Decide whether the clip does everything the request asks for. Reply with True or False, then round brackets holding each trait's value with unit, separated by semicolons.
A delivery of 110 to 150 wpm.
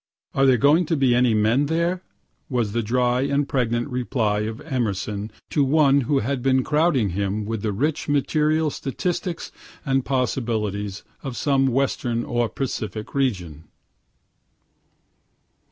True (135 wpm)